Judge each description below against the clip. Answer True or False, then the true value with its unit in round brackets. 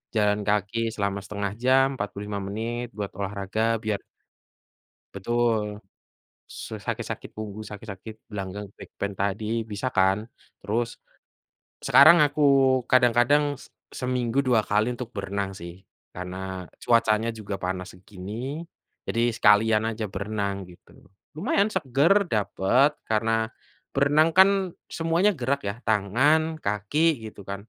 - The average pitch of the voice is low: True (110 Hz)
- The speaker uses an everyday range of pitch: True (4.0 semitones)